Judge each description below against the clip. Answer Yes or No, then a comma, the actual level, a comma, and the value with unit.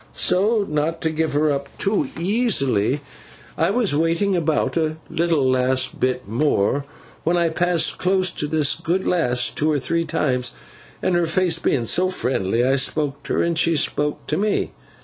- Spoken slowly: No, average, 175 wpm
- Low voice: No, medium, 155 Hz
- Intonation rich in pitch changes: No, average, 4.1 semitones